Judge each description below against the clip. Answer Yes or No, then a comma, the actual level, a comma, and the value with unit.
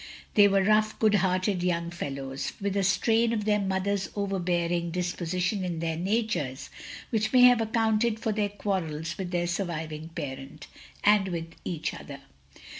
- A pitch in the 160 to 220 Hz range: Yes, medium, 185 Hz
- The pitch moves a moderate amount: Yes, average, 3.7 semitones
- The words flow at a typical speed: Yes, average, 160 wpm